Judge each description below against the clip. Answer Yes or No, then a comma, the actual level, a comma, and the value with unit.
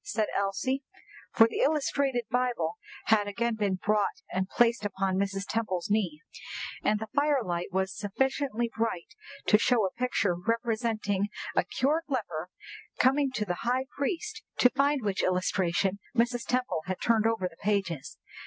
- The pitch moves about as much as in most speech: Yes, average, 4.5 semitones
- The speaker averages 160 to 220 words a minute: No, average, 150 wpm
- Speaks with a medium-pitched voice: No, high, 220 Hz